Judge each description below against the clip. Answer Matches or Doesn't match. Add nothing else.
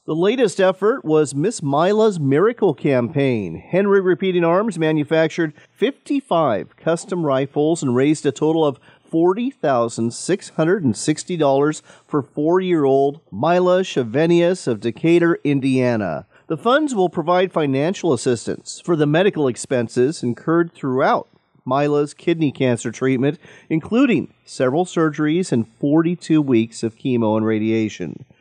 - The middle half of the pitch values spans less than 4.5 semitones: Doesn't match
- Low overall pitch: Doesn't match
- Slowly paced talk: Matches